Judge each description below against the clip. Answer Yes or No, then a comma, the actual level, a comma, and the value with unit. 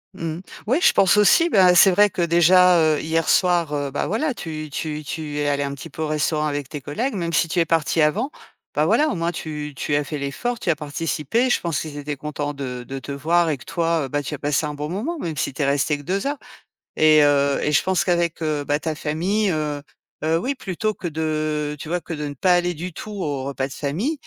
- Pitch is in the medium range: Yes, medium, 155 Hz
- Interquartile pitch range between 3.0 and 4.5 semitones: Yes, average, 3.3 semitones